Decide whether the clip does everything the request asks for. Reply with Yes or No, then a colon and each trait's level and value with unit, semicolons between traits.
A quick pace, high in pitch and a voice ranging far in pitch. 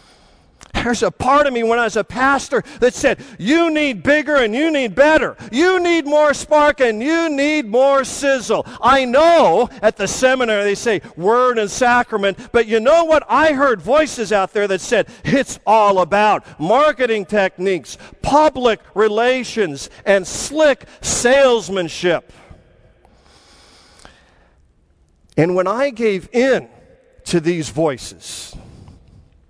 No: slow, 135 wpm; high, 240 Hz; wide, 6.3 semitones